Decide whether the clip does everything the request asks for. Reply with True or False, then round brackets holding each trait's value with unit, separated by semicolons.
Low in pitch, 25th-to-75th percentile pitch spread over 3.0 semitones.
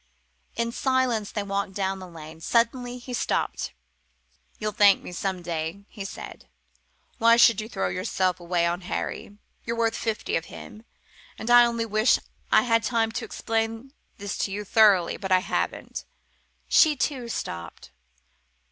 False (215 Hz; 3.7 semitones)